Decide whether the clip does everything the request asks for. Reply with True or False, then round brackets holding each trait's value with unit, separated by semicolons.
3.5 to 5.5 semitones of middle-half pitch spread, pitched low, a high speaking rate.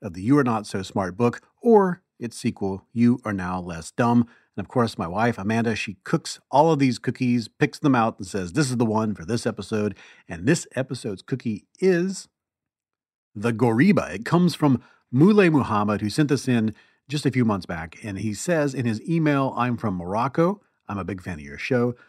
True (5.0 semitones; 120 Hz; 210 wpm)